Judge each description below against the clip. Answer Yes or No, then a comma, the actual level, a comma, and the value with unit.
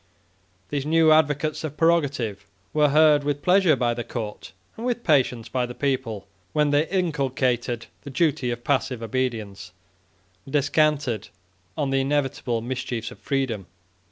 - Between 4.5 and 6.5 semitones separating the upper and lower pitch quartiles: No, average, 4.0 semitones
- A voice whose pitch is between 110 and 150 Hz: Yes, low, 135 Hz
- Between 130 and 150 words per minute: Yes, average, 145 wpm